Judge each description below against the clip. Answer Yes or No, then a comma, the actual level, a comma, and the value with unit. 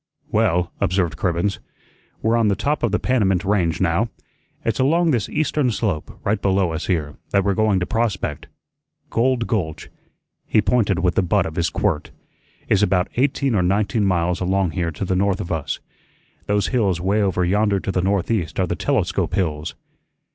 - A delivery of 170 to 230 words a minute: Yes, average, 180 wpm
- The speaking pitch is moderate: No, very low, 95 Hz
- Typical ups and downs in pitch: Yes, average, 3.7 semitones